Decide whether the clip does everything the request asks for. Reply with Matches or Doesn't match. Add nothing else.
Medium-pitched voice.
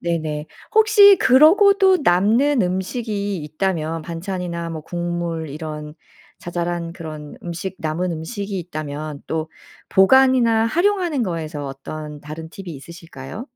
Matches